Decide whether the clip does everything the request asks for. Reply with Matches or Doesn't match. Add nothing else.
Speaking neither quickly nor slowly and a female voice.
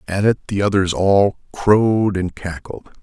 Doesn't match